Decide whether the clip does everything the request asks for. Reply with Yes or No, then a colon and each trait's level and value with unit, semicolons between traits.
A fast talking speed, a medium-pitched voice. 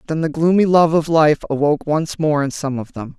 Yes: fast, 245 wpm; medium, 155 Hz